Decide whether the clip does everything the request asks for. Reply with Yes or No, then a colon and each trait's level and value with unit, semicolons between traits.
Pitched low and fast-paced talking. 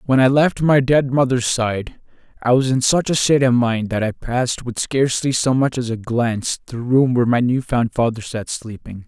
Yes: low, 125 Hz; fast, 225 wpm